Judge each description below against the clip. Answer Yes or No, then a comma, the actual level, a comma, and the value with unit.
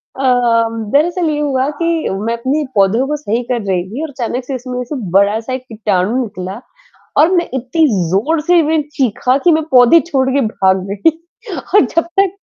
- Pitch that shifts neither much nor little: No, wide, 5.9 semitones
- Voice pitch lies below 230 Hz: No, very high, 260 Hz